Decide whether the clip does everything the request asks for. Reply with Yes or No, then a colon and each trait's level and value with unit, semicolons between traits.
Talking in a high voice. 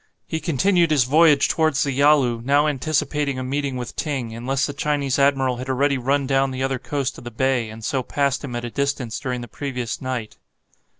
No: low, 135 Hz